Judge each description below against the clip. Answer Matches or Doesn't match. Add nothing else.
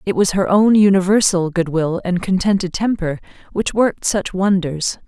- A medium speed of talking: Matches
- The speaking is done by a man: Doesn't match